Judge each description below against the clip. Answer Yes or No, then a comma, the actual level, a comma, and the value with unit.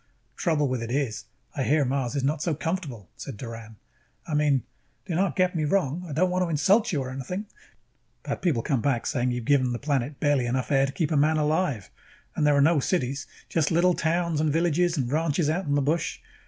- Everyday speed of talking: No, fast, 230 wpm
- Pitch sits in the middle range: Yes, medium, 145 Hz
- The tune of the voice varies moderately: Yes, average, 3.9 semitones